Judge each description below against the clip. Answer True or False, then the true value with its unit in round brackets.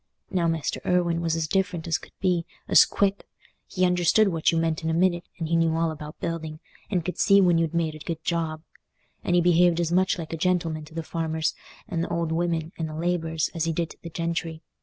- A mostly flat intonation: True (1.4 semitones)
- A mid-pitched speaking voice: True (165 Hz)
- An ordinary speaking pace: False (230 wpm)